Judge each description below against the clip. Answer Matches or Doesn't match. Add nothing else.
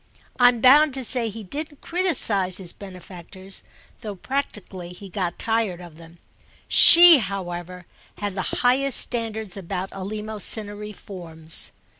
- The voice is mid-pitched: Doesn't match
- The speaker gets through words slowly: Matches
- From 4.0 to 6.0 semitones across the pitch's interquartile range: Matches